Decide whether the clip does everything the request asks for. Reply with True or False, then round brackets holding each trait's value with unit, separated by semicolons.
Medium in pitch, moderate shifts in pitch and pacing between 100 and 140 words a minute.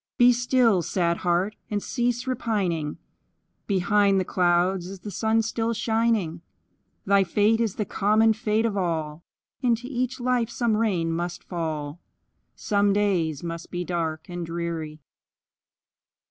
False (200 Hz; 4.7 semitones; 135 wpm)